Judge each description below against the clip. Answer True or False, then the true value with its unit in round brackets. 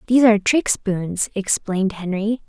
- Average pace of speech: True (145 wpm)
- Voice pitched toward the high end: True (205 Hz)